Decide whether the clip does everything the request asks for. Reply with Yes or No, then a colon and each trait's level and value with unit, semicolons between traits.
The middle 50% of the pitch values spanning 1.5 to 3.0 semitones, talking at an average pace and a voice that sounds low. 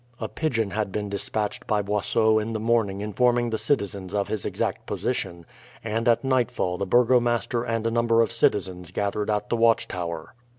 Yes: narrow, 2.6 semitones; average, 175 wpm; low, 110 Hz